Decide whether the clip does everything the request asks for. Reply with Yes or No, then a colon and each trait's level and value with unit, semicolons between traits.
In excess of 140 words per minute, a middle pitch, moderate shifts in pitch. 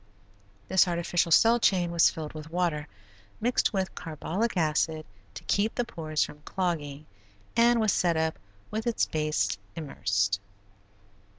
No: slow, 135 wpm; medium, 170 Hz; average, 4.0 semitones